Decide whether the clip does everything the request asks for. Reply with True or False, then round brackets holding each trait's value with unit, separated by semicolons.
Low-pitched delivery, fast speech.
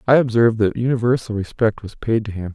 True (115 Hz; 210 wpm)